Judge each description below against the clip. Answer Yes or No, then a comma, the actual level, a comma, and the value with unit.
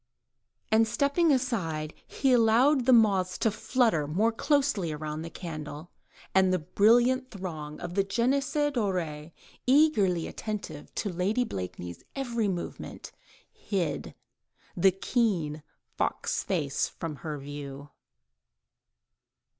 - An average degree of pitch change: No, wide, 7.5 semitones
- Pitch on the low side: No, high, 195 Hz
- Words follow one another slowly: Yes, slow, 115 wpm